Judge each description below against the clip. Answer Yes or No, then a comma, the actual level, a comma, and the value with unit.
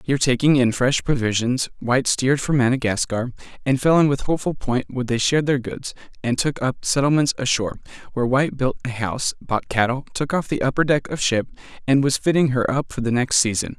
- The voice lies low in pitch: Yes, low, 130 Hz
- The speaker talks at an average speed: No, fast, 210 wpm